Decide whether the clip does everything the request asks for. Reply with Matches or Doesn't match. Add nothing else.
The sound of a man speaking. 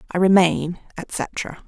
Doesn't match